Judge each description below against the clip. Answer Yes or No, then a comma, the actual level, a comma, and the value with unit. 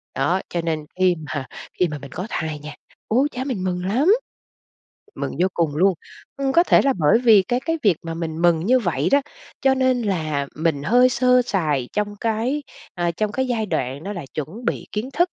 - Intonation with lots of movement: Yes, wide, 7.6 semitones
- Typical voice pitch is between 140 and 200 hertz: Yes, high, 190 Hz